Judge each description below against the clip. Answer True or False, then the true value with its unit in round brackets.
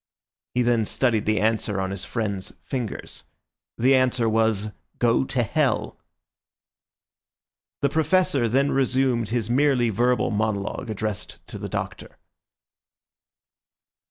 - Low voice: True (120 Hz)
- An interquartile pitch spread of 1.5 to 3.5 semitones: True (3.2 semitones)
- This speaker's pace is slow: True (115 wpm)